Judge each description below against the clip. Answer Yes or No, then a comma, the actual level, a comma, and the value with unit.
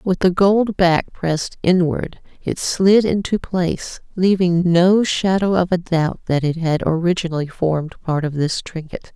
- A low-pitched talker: No, medium, 175 Hz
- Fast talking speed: No, average, 155 wpm